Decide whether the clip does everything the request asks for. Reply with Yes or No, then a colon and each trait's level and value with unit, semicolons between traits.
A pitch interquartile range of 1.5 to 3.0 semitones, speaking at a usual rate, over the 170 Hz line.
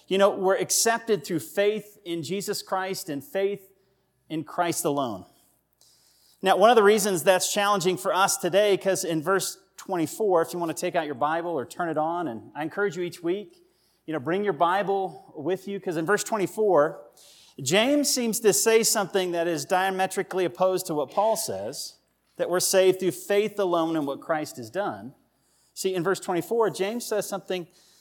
Yes: average, 2.7 semitones; average, 190 wpm; high, 190 Hz